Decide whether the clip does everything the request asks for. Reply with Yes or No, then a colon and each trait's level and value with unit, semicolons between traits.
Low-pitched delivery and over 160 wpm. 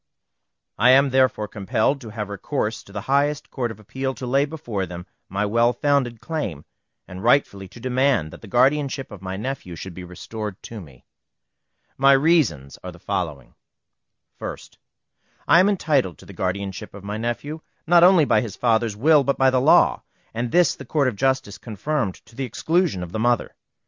Yes: low, 120 Hz; average, 185 wpm